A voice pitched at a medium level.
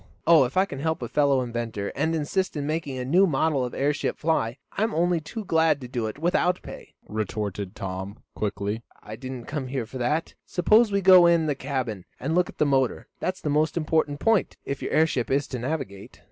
Yes: medium, 145 Hz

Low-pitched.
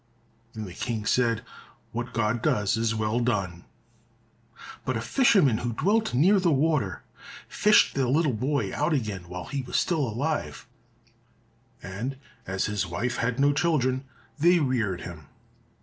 Yes: low, 120 Hz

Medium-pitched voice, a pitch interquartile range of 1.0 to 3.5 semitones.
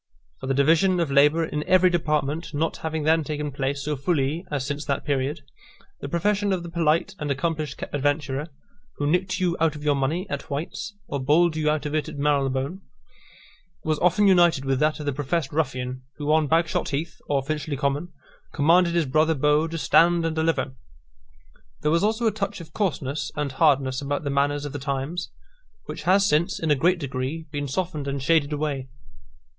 Yes: medium, 150 Hz; average, 3.1 semitones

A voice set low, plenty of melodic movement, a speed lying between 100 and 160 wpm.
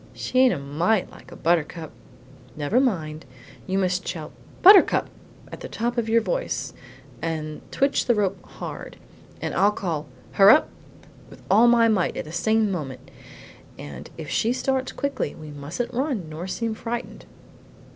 No: high, 195 Hz; wide, 7.1 semitones; average, 155 wpm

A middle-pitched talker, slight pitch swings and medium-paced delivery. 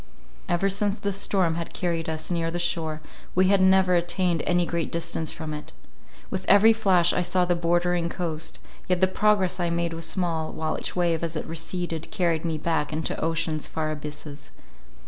Yes: medium, 170 Hz; narrow, 2.1 semitones; average, 185 wpm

